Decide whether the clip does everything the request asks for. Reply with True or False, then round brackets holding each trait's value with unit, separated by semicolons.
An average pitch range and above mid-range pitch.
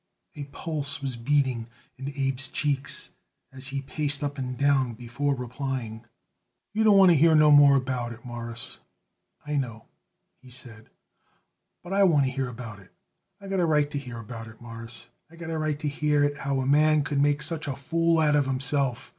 False (3.1 semitones; 140 Hz)